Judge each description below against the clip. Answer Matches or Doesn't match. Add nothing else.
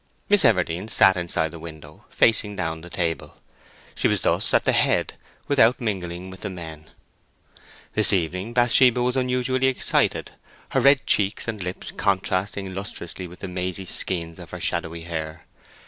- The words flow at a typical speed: Matches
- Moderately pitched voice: Doesn't match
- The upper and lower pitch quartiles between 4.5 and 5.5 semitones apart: Matches